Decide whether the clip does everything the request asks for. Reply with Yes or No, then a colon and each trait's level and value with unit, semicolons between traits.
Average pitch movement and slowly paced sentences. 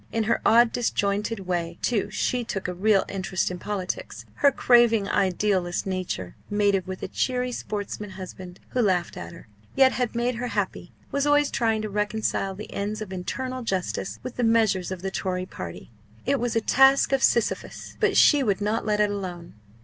No: average, 4.1 semitones; average, 190 wpm